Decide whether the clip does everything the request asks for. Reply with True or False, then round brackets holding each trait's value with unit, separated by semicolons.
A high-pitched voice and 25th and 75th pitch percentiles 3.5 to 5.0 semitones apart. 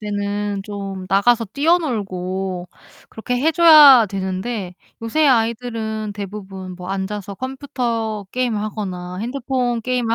True (215 Hz; 4.2 semitones)